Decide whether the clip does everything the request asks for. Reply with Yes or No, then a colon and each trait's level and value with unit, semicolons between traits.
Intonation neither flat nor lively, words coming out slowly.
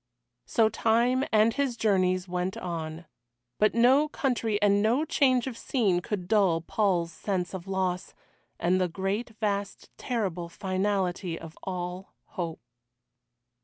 Yes: average, 3.9 semitones; slow, 130 wpm